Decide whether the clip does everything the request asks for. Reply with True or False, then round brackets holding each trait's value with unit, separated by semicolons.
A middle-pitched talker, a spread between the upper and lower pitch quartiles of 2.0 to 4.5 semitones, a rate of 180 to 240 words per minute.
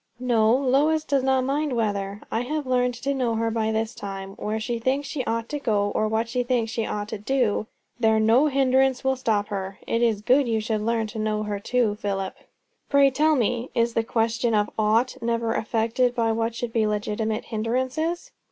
False (230 Hz; 3.0 semitones; 205 wpm)